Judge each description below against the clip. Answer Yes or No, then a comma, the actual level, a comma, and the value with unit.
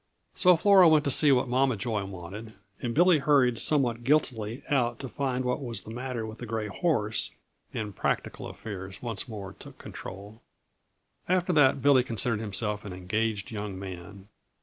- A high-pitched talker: No, low, 115 Hz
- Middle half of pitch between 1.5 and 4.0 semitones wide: No, average, 4.6 semitones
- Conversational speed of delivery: Yes, average, 170 wpm